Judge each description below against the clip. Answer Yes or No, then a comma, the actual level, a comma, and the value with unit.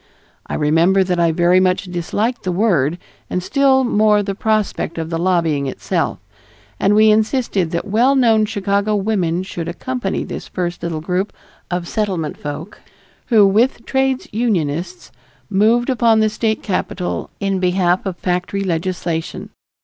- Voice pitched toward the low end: No, high, 190 Hz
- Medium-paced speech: Yes, average, 150 wpm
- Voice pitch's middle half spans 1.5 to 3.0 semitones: No, average, 3.9 semitones